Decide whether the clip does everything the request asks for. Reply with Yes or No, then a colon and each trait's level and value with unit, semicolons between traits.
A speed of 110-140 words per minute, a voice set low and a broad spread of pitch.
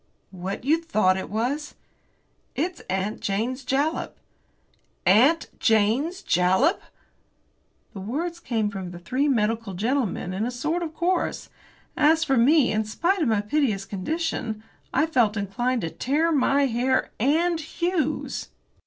No: slow, 135 wpm; very high, 255 Hz; wide, 6.9 semitones